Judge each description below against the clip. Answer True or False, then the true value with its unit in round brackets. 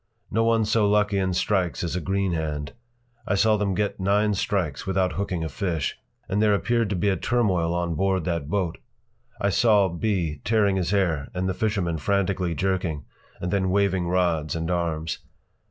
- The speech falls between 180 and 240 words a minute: True (185 wpm)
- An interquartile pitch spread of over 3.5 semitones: False (3.0 semitones)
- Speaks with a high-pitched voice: False (95 Hz)